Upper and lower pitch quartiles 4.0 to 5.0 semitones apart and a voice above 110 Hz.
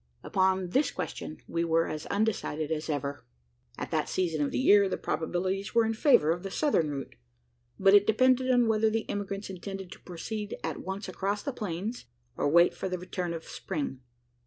Yes: average, 4.3 semitones; high, 190 Hz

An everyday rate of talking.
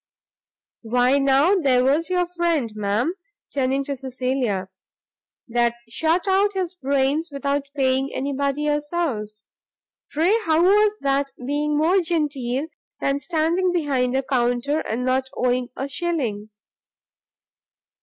No: slow, 125 wpm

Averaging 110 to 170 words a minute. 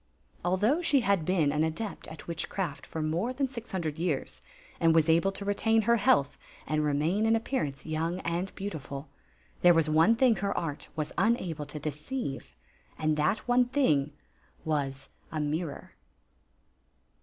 Yes: average, 165 wpm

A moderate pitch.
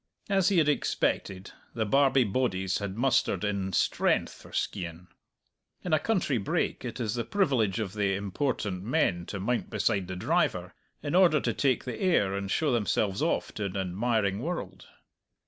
No: low, 110 Hz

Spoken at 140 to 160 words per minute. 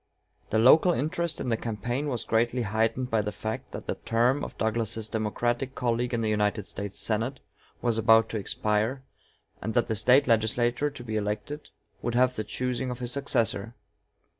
No: average, 180 wpm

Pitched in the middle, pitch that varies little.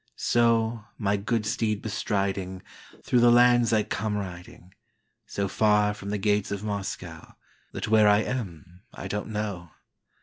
No: low, 105 Hz; narrow, 2.1 semitones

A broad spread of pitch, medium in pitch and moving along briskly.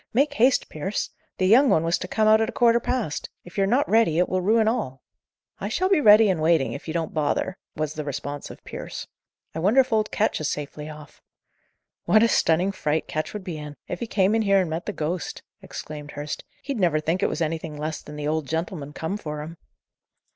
Yes: wide, 6.0 semitones; medium, 170 Hz; fast, 230 wpm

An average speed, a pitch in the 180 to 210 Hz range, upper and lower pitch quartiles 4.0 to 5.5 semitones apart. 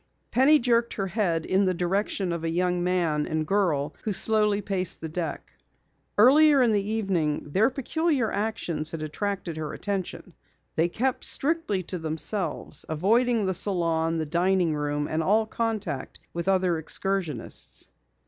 Yes: average, 150 wpm; medium, 185 Hz; average, 4.9 semitones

